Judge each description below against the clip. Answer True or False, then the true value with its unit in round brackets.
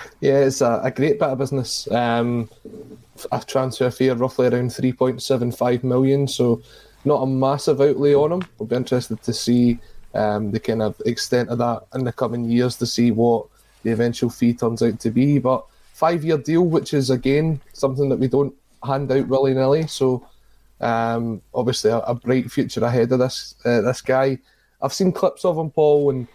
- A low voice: True (130 Hz)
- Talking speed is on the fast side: False (180 wpm)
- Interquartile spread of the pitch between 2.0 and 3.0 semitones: True (2.4 semitones)